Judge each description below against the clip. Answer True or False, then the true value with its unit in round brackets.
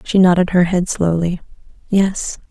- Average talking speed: True (145 wpm)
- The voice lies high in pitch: False (180 Hz)